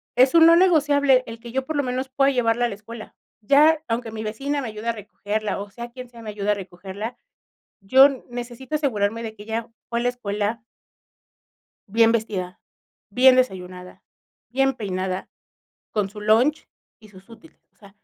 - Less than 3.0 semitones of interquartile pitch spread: No, average, 3.8 semitones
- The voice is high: Yes, high, 230 Hz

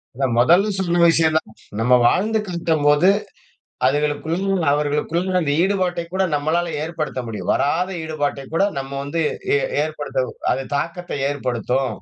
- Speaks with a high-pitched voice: No, medium, 155 Hz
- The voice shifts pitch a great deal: No, average, 3.5 semitones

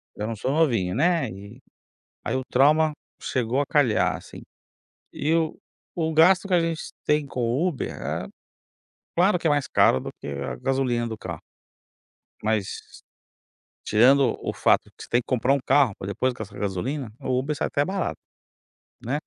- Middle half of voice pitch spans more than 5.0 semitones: Yes, wide, 5.4 semitones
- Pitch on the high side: No, low, 130 Hz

